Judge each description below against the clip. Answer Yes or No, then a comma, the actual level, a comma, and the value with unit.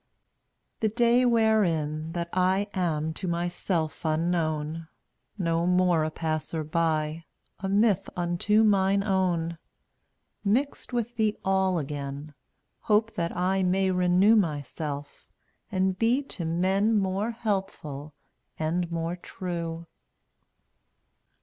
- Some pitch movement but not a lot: Yes, average, 3.5 semitones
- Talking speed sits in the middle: No, slow, 115 wpm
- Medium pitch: Yes, medium, 180 Hz